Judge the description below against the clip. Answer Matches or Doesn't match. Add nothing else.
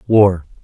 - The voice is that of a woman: Doesn't match